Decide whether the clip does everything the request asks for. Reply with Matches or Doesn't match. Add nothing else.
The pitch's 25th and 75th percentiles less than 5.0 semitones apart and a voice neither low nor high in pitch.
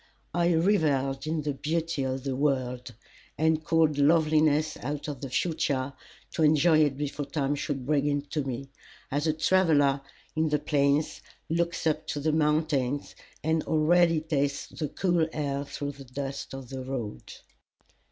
Matches